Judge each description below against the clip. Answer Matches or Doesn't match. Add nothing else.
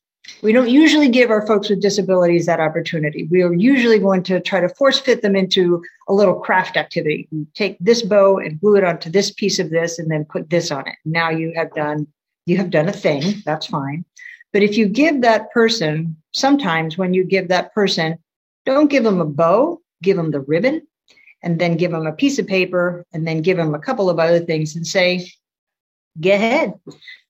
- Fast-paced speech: Matches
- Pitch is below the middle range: Doesn't match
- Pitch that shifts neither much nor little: Matches